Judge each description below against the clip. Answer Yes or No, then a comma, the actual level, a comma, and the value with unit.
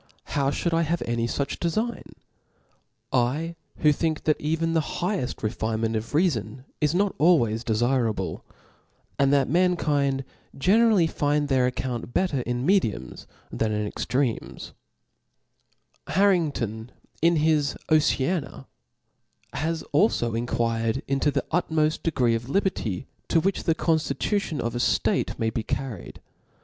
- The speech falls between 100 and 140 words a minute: Yes, slow, 135 wpm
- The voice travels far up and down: Yes, wide, 5.8 semitones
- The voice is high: No, medium, 140 Hz